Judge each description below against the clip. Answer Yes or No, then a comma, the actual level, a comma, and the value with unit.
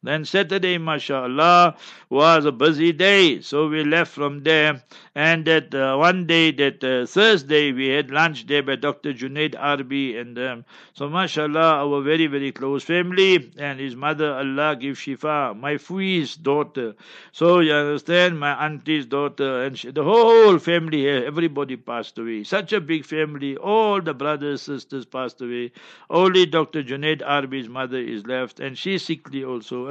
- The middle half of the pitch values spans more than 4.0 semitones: No, average, 3.2 semitones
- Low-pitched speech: No, medium, 150 Hz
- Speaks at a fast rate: No, average, 165 wpm